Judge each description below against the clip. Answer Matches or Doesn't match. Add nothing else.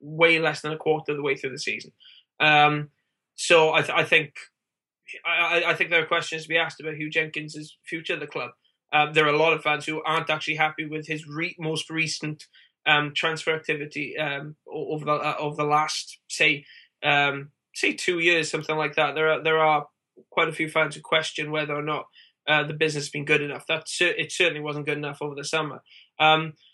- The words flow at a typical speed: Doesn't match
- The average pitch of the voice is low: Doesn't match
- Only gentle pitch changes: Matches